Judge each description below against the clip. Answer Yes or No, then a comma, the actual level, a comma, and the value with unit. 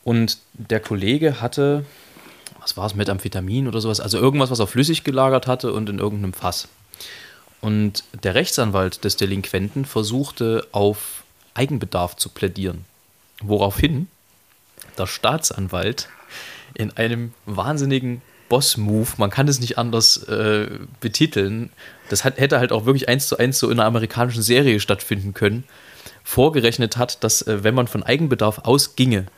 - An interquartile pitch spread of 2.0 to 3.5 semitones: No, average, 4.0 semitones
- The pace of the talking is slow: No, average, 145 wpm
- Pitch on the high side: No, low, 115 Hz